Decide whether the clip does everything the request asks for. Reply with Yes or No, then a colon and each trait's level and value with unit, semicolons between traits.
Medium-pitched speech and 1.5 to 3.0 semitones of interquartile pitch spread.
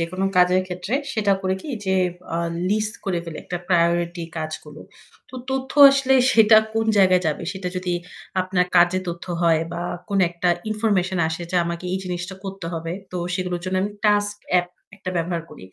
Yes: medium, 180 Hz; narrow, 2.5 semitones